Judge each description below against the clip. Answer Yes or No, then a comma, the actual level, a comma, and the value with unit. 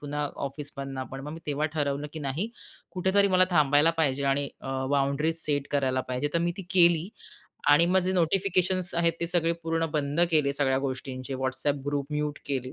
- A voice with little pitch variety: No, average, 3.3 semitones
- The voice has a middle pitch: Yes, medium, 150 Hz